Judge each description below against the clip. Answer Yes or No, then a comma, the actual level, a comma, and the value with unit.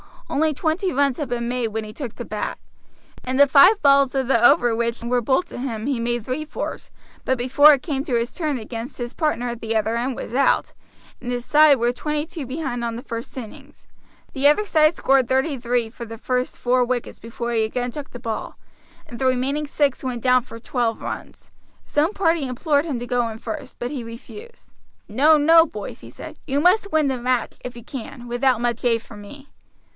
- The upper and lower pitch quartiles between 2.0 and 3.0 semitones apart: No, average, 3.4 semitones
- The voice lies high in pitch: Yes, very high, 255 Hz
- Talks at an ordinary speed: No, fast, 220 wpm